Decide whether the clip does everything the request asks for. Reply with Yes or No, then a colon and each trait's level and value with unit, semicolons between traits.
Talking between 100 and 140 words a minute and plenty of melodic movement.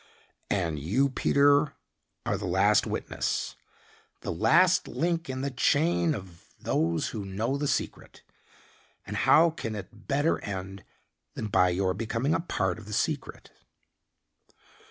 Yes: slow, 135 wpm; wide, 7.2 semitones